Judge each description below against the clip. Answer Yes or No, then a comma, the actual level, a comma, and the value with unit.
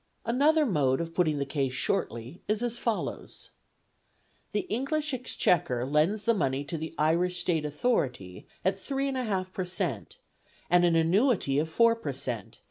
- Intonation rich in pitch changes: Yes, wide, 8.1 semitones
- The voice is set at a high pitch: No, medium, 175 Hz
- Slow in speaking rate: No, average, 155 wpm